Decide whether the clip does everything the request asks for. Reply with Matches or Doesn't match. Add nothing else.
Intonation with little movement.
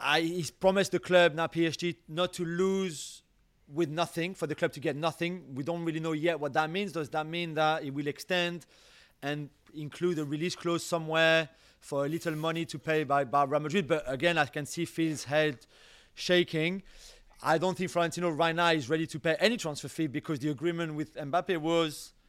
Matches